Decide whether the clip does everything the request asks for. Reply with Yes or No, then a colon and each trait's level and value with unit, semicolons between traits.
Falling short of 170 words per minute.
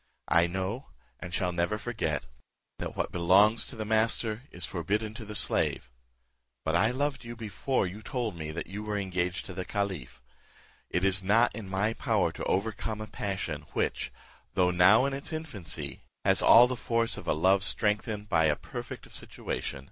No: average, 185 wpm